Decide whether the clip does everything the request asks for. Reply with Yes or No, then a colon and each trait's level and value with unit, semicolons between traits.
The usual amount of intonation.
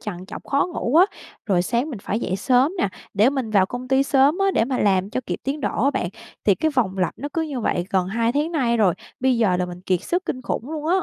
No: wide, 6.4 semitones